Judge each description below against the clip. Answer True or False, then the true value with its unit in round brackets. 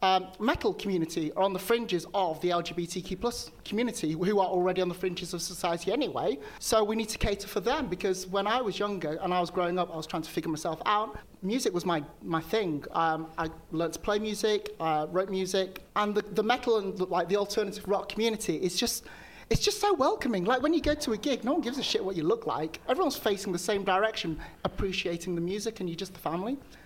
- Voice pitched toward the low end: False (190 Hz)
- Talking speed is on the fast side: True (245 wpm)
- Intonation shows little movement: False (3.8 semitones)